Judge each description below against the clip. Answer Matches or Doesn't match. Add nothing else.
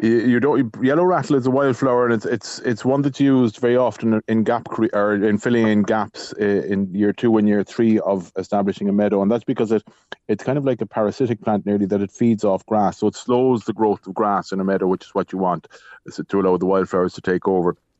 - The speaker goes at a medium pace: Doesn't match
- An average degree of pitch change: Matches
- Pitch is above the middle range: Doesn't match